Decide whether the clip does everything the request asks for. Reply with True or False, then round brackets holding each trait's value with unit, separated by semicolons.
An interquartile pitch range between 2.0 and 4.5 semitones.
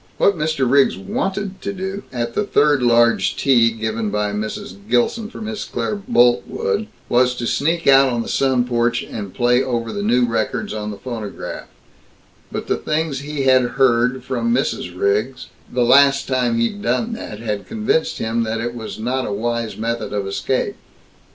True (3.6 semitones)